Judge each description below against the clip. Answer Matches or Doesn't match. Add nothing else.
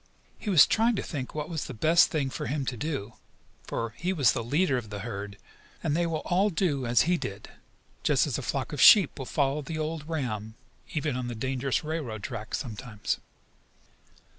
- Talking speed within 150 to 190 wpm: Doesn't match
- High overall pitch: Doesn't match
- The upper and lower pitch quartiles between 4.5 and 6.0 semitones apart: Matches